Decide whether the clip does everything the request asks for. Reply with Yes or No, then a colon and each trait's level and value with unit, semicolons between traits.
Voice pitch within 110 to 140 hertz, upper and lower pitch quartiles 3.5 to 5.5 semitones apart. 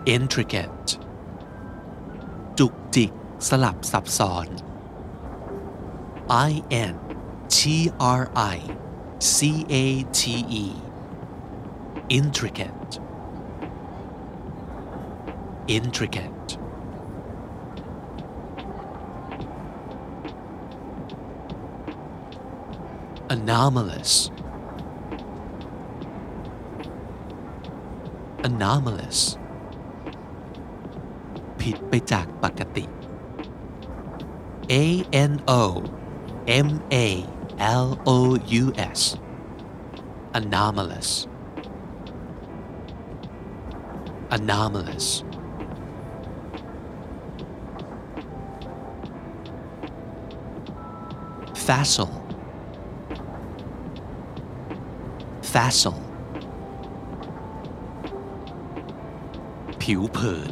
Yes: low, 115 Hz; average, 4.7 semitones